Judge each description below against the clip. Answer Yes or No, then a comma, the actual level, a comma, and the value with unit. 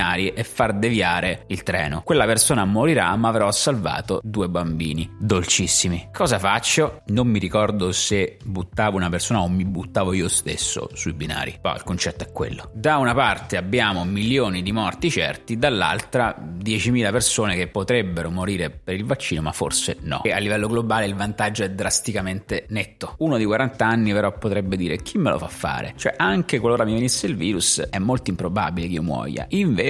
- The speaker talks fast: Yes, fast, 180 wpm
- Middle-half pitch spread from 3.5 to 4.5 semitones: Yes, average, 3.8 semitones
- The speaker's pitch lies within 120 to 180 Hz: No, low, 100 Hz